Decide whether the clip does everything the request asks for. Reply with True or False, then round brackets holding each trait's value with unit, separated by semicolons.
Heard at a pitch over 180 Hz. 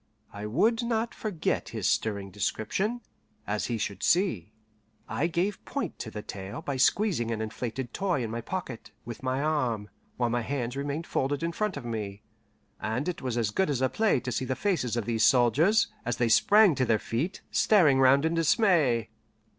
False (130 Hz)